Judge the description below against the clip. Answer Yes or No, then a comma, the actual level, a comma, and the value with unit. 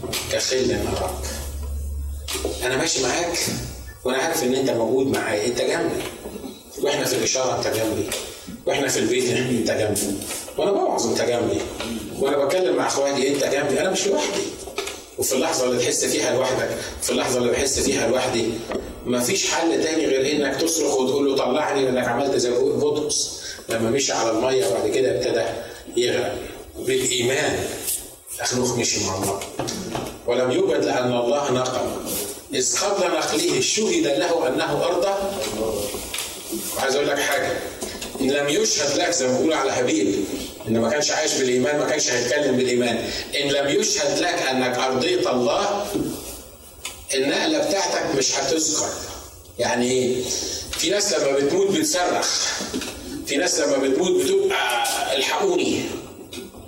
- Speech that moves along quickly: Yes, fast, 140 wpm